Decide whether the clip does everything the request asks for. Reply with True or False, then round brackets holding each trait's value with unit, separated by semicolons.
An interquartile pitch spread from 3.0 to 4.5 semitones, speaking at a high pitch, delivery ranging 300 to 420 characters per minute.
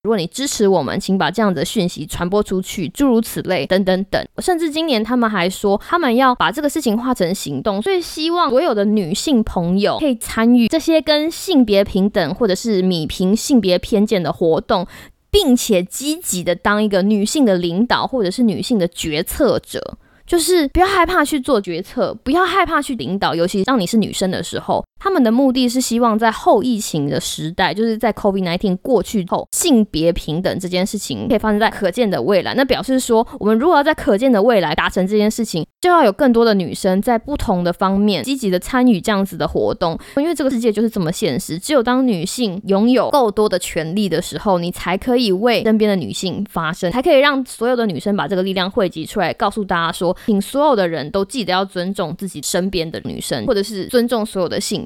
False (5.3 semitones; 210 Hz; 335 characters per minute)